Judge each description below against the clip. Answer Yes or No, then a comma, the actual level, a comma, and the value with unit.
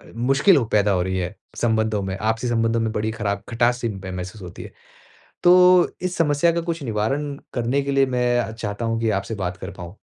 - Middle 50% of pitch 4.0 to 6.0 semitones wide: Yes, average, 5.2 semitones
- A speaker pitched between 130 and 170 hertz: No, low, 115 Hz